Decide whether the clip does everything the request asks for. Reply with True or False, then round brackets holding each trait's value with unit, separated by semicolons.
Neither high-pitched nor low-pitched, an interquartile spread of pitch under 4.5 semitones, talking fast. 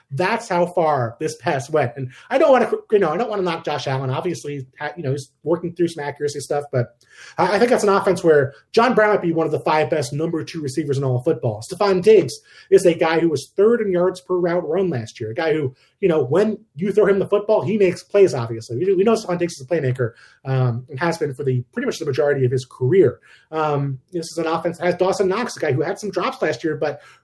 False (165 Hz; 5.0 semitones; 260 wpm)